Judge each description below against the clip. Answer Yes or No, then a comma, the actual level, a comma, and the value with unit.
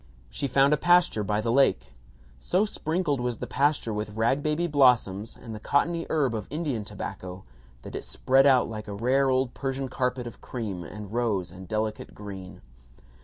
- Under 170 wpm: No, average, 180 wpm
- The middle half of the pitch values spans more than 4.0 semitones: Yes, average, 4.8 semitones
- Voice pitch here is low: Yes, low, 125 Hz